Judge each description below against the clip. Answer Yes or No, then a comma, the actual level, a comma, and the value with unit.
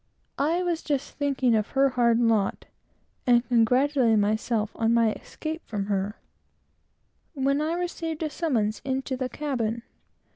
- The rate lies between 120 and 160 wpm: Yes, average, 140 wpm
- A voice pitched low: No, very high, 250 Hz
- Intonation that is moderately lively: Yes, average, 4.5 semitones